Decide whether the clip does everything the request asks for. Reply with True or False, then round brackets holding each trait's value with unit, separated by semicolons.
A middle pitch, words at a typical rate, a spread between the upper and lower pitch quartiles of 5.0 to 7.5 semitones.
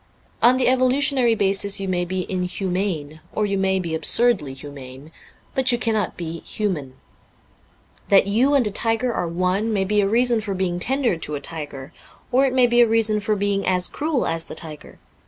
False (195 Hz; 190 wpm; 5.3 semitones)